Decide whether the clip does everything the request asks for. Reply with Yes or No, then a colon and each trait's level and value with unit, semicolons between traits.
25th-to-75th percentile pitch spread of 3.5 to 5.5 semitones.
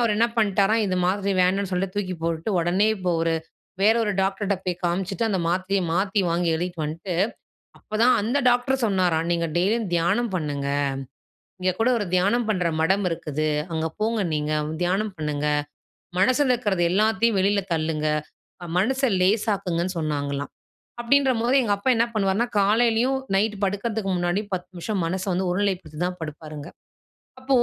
Yes: average, 3.9 semitones